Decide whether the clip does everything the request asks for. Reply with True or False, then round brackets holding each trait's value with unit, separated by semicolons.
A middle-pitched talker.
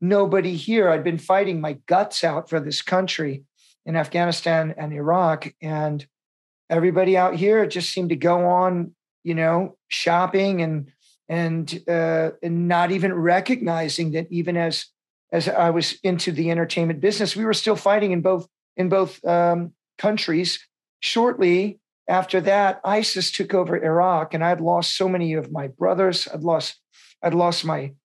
True (175 Hz)